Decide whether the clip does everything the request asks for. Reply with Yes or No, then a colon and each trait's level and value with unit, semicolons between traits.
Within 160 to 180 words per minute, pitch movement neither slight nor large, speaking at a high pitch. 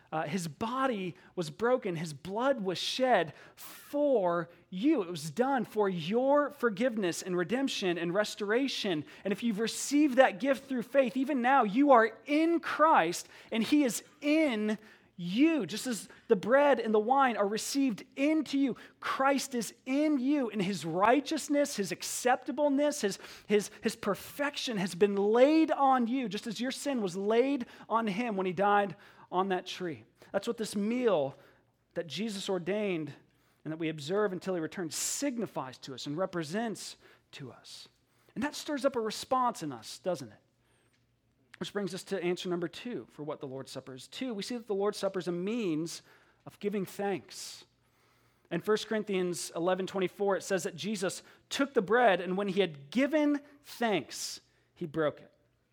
No: average, 175 wpm; wide, 6.7 semitones; high, 205 Hz